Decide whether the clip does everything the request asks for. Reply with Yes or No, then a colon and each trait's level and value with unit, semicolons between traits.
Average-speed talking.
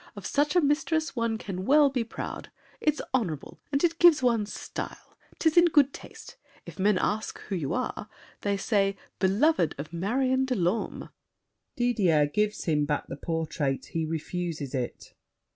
Yes: average, 160 wpm